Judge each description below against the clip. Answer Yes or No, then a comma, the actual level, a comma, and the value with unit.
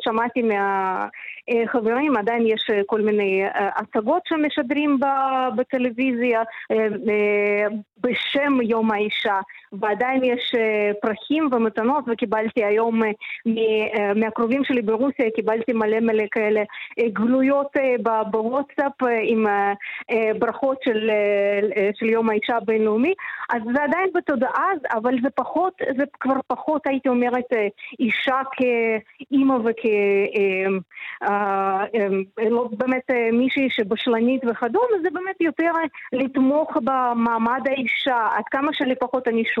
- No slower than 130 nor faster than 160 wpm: No, average, 105 wpm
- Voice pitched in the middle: No, high, 235 Hz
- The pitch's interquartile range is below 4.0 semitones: Yes, average, 3.5 semitones